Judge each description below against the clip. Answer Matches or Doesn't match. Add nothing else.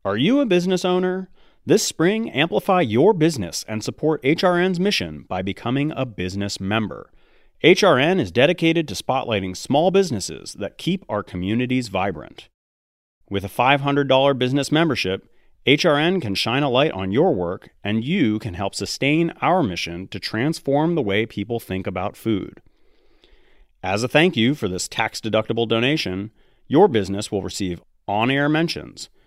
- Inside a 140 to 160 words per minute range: Matches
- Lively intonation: Matches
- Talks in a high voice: Doesn't match